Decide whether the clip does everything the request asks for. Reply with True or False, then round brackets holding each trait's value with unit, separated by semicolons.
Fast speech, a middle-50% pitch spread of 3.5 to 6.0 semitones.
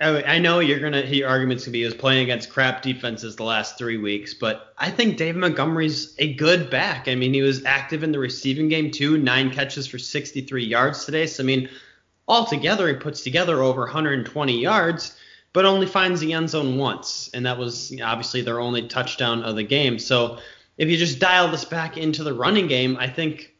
True (210 wpm; 4.0 semitones)